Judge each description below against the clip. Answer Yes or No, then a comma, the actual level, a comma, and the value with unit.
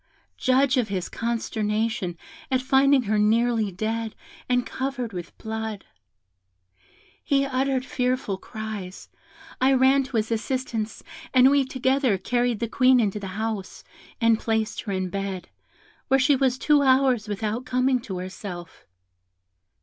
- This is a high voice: Yes, high, 230 Hz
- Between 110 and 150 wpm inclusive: Yes, slow, 135 wpm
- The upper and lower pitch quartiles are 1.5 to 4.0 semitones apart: Yes, average, 3.7 semitones